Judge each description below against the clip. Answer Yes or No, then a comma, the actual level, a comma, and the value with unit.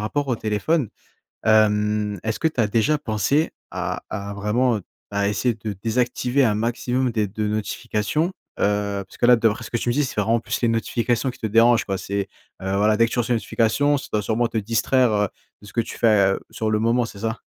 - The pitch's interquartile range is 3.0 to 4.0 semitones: No, narrow, 2.5 semitones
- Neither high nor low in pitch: No, low, 110 Hz